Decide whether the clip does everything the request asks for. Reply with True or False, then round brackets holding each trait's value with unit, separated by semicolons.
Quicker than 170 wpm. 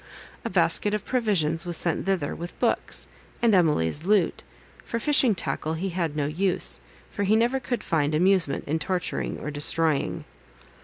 False (160 wpm)